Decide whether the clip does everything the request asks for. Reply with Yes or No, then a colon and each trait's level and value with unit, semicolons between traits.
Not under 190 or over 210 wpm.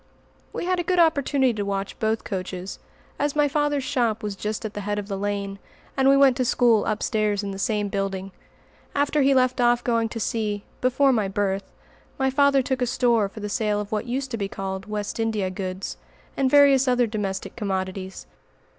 Yes: average, 200 wpm